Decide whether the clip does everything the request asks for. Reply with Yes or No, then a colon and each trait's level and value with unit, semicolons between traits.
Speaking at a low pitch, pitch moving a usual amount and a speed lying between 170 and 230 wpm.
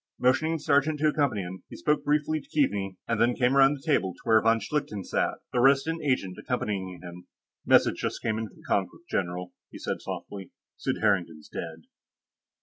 No: low, 115 Hz; wide, 7.3 semitones; average, 190 wpm